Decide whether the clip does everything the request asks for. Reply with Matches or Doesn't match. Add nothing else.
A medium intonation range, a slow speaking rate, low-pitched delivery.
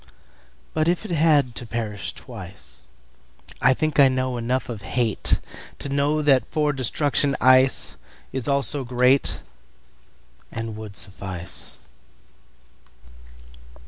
Matches